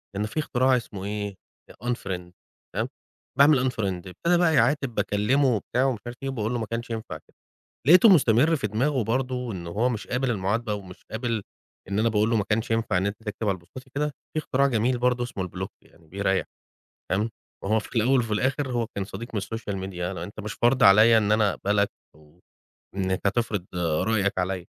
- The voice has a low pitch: Yes, low, 110 Hz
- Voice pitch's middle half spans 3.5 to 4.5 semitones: Yes, average, 4.1 semitones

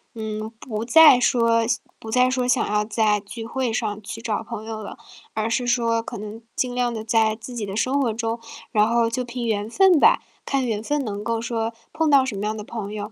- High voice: Yes, high, 230 Hz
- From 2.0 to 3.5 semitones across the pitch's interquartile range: Yes, narrow, 2.4 semitones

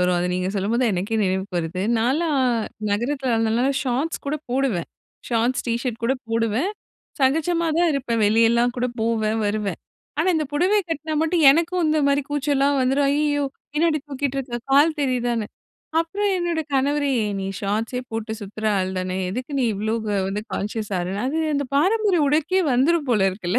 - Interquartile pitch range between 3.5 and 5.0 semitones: No, wide, 5.5 semitones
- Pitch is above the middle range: Yes, very high, 255 Hz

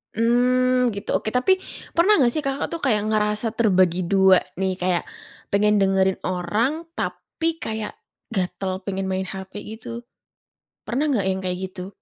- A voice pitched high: Yes, high, 210 Hz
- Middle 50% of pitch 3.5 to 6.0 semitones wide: Yes, average, 4.1 semitones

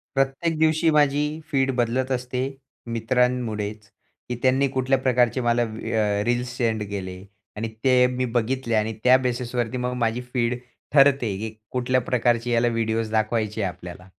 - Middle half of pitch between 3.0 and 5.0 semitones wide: No, narrow, 2.5 semitones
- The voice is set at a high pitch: No, low, 120 Hz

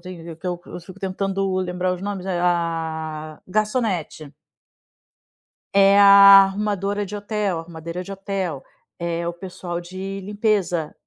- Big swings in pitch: No, narrow, 2.5 semitones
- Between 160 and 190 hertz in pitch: Yes, medium, 185 Hz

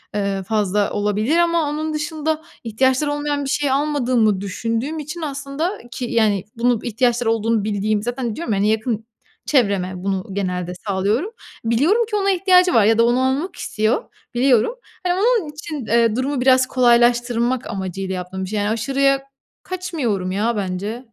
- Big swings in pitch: Yes, wide, 5.8 semitones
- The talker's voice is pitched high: Yes, high, 240 Hz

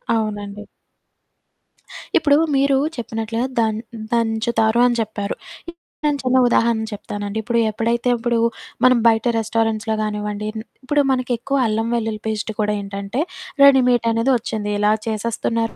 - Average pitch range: No, narrow, 2.0 semitones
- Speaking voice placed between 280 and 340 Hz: No, high, 225 Hz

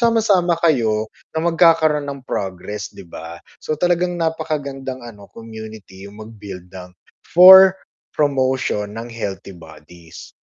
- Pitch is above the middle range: No, low, 125 Hz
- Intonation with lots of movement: Yes, wide, 8.3 semitones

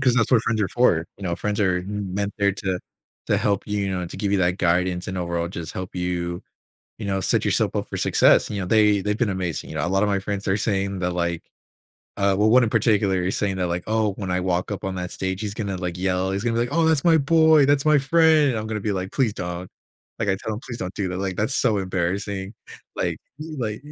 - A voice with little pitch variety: No, average, 3.0 semitones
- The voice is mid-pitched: No, low, 100 Hz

